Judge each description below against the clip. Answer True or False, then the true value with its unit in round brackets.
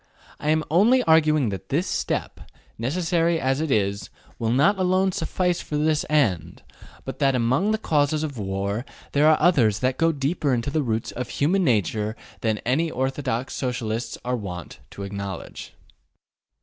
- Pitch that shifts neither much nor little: False (6.3 semitones)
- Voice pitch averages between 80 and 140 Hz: True (135 Hz)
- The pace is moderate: True (165 wpm)